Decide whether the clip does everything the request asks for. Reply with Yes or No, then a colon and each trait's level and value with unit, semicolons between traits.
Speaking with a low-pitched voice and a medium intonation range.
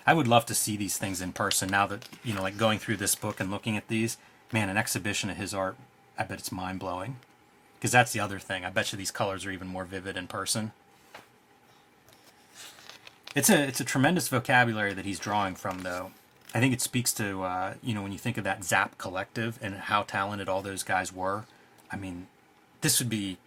Yes: low, 100 Hz; average, 3.0 semitones